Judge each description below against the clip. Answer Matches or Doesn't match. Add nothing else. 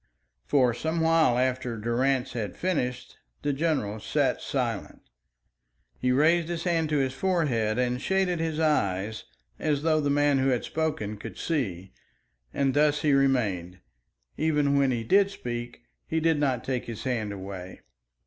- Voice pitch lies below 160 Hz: Matches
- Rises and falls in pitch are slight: Doesn't match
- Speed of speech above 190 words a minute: Doesn't match